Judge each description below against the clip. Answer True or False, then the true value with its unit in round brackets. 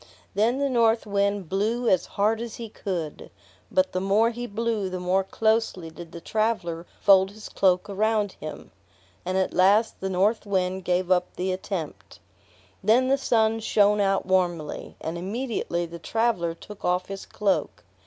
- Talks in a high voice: True (195 Hz)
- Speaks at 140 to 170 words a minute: True (165 wpm)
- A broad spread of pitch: False (3.4 semitones)